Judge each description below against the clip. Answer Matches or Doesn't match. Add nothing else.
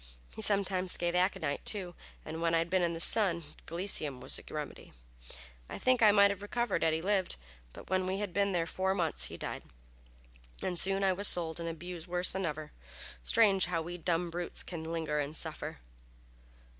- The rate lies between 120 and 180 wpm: Doesn't match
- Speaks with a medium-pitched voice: Matches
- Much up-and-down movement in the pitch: Doesn't match